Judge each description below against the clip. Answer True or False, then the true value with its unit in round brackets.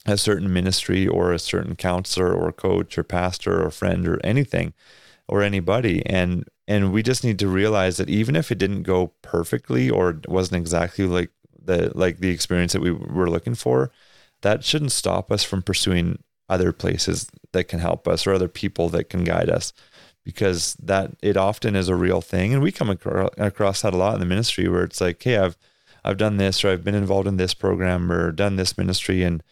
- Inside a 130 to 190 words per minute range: False (205 wpm)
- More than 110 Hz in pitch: False (95 Hz)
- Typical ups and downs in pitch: False (2.3 semitones)